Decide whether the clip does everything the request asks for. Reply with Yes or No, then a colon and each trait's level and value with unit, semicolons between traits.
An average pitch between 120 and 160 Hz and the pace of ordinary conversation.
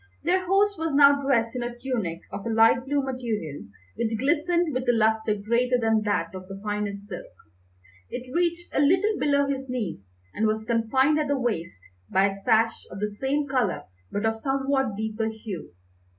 No: high, 235 Hz; average, 185 wpm